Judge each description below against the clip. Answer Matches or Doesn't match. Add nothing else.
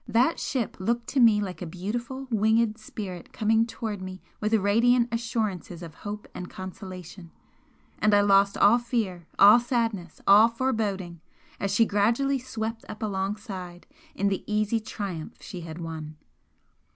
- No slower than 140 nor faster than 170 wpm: Matches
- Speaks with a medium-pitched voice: Doesn't match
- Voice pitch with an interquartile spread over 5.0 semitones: Doesn't match